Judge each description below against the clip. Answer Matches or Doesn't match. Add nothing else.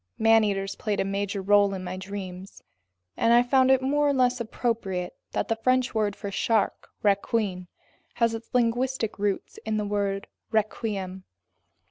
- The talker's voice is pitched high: Matches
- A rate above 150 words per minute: Matches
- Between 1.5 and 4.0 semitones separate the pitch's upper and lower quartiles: Matches